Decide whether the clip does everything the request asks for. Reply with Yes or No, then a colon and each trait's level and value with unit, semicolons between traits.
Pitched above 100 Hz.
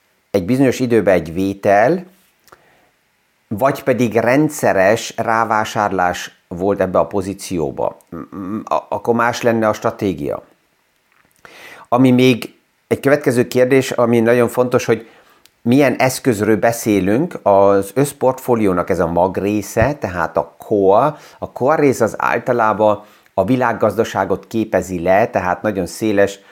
Yes: low, 115 Hz